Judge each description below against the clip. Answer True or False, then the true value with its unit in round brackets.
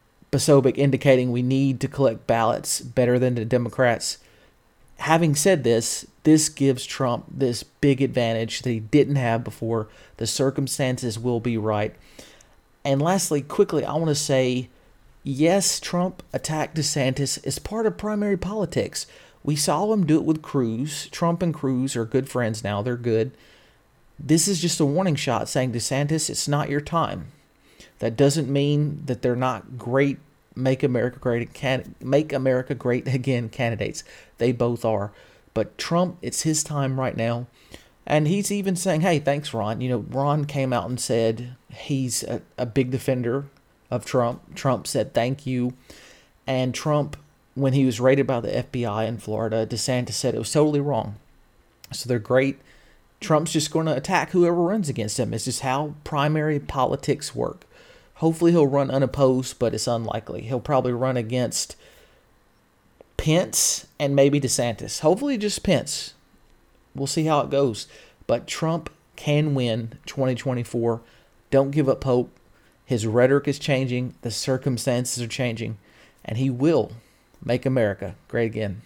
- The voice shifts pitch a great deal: False (3.6 semitones)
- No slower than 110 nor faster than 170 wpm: True (160 wpm)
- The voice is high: False (130 Hz)